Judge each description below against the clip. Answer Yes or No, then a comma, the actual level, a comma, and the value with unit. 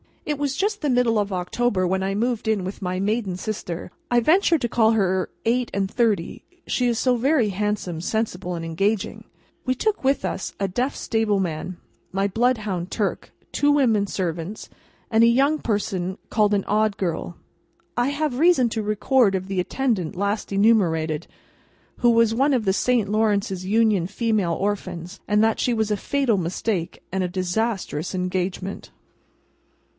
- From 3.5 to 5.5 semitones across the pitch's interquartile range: Yes, average, 4.2 semitones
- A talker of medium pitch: No, high, 210 Hz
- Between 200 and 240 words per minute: No, average, 165 wpm